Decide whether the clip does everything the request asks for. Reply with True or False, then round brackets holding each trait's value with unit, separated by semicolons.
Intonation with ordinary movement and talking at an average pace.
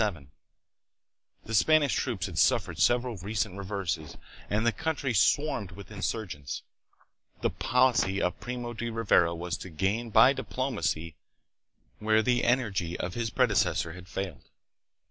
False (5.0 semitones; 130 wpm)